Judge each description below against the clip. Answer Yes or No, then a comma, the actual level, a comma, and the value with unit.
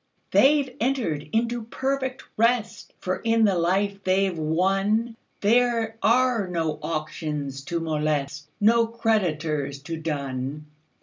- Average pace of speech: No, slow, 110 wpm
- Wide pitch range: Yes, wide, 6.9 semitones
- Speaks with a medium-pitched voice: No, high, 195 Hz